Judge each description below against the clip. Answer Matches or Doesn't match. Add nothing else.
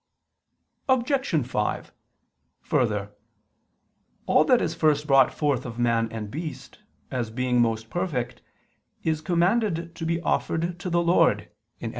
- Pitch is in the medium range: Matches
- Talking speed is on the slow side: Matches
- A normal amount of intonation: Doesn't match